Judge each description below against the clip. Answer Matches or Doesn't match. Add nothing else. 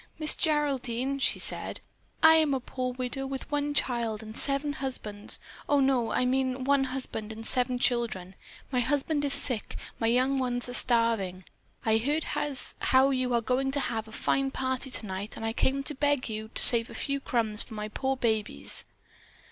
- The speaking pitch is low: Doesn't match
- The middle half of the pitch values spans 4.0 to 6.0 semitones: Doesn't match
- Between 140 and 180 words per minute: Doesn't match